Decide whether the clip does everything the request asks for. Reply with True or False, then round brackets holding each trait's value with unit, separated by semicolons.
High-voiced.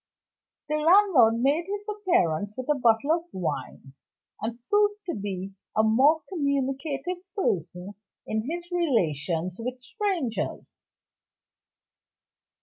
True (270 Hz)